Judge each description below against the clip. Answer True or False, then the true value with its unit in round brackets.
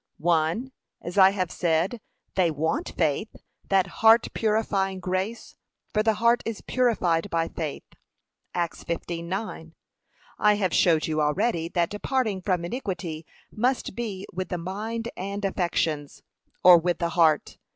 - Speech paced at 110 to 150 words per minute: True (140 wpm)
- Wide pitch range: False (4.1 semitones)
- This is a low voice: False (185 Hz)